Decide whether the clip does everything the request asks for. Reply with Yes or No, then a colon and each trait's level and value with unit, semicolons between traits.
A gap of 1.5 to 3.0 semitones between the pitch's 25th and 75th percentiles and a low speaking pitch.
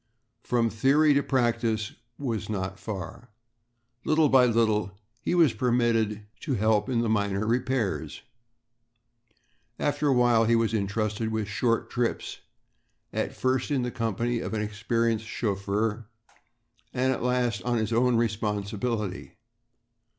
Yes: narrow, 2.6 semitones; low, 115 Hz